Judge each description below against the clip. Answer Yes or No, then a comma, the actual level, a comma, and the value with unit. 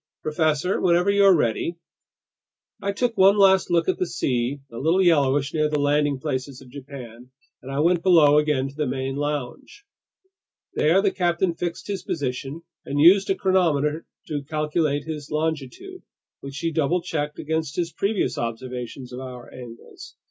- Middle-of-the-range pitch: Yes, medium, 150 Hz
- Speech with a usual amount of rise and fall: Yes, average, 4.2 semitones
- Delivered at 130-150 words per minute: No, average, 165 wpm